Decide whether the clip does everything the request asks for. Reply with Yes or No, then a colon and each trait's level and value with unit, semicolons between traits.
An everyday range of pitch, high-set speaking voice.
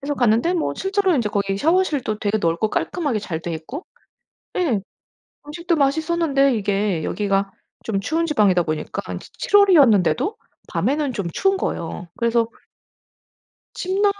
No: wide, 8.9 semitones; very high, 255 Hz